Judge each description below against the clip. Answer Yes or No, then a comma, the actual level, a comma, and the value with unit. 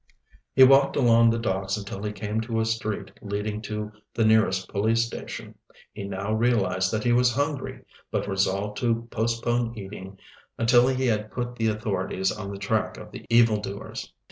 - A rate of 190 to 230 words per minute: No, average, 170 wpm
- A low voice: Yes, low, 110 Hz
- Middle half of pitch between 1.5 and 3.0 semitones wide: Yes, average, 2.7 semitones